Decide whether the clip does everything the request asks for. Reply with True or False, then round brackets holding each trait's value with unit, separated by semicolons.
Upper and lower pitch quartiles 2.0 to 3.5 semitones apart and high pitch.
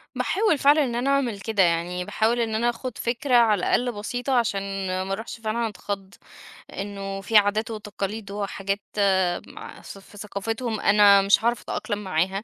True (3.0 semitones; 215 Hz)